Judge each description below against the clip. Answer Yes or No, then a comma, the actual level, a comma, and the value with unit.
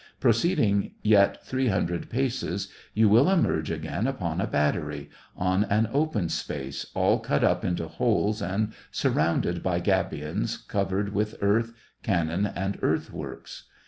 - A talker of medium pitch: No, low, 100 Hz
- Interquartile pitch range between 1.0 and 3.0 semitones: No, average, 4.4 semitones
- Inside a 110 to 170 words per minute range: Yes, average, 145 wpm